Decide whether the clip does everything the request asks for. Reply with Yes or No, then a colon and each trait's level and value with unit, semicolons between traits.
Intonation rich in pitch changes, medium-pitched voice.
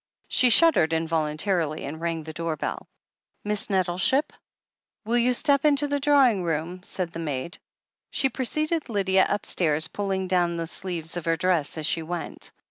Yes: wide, 6.4 semitones; medium, 180 Hz